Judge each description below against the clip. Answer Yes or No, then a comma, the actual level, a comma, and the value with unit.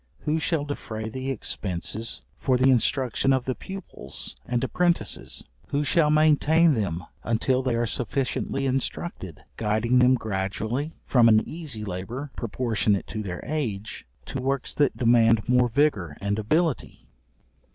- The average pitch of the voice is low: Yes, low, 125 Hz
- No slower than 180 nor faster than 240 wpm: No, average, 140 wpm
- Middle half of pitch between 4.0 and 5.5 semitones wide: Yes, average, 4.6 semitones